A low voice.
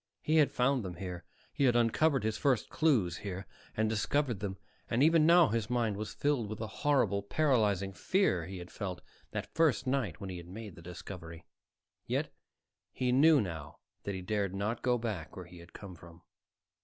Yes: low, 105 Hz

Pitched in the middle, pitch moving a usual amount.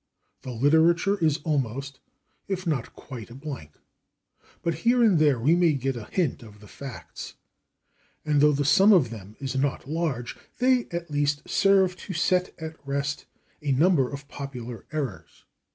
Yes: medium, 145 Hz; average, 4.3 semitones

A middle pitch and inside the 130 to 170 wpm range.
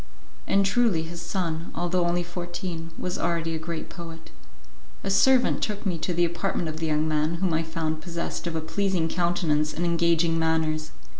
No: medium, 170 Hz; average, 180 wpm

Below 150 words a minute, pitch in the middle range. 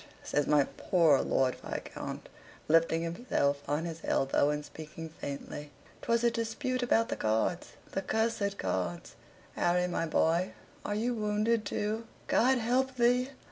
Yes: average, 140 wpm; medium, 180 Hz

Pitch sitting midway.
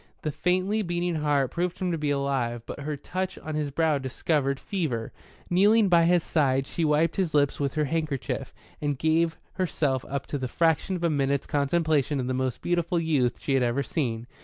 Yes: medium, 150 Hz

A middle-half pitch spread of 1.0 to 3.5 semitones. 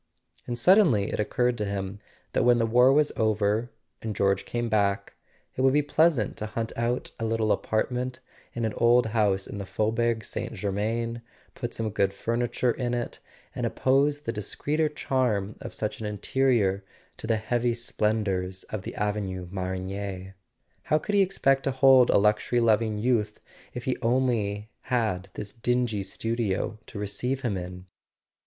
Yes: average, 3.2 semitones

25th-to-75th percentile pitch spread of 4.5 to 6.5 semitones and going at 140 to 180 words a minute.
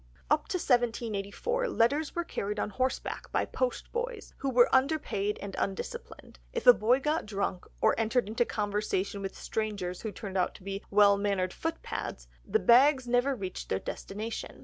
Yes: wide, 5.4 semitones; average, 170 wpm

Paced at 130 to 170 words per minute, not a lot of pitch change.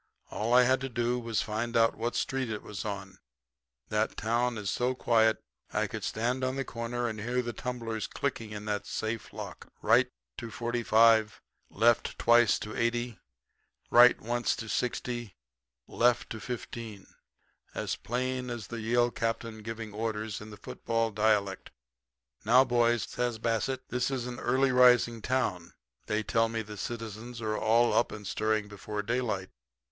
Yes: average, 165 wpm; narrow, 2.0 semitones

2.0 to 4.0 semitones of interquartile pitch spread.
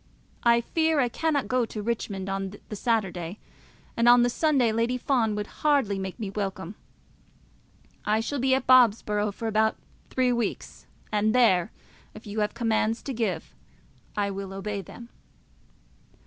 Yes: average, 3.2 semitones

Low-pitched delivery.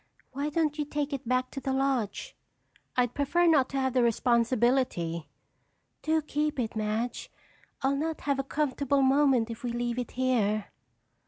No: very high, 260 Hz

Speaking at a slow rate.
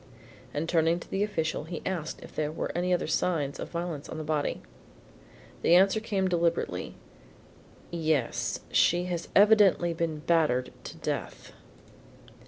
No: average, 145 wpm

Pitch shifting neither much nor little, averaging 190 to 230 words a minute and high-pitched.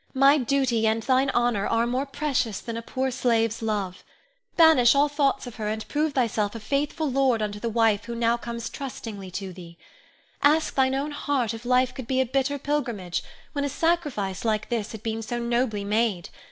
Yes: average, 3.8 semitones; average, 195 wpm; high, 240 Hz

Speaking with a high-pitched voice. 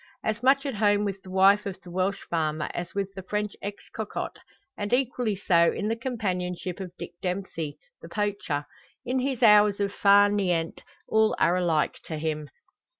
Yes: high, 200 Hz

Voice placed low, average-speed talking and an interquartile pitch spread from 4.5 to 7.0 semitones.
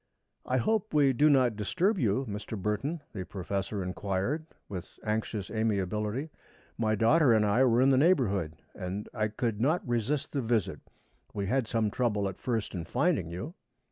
Yes: low, 110 Hz; average, 170 wpm; average, 4.8 semitones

